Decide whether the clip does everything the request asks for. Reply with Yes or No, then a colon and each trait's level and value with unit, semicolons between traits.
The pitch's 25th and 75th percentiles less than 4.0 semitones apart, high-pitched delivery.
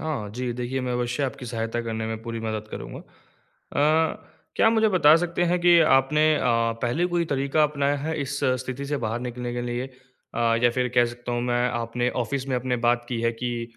No: average, 3.4 semitones; low, 125 Hz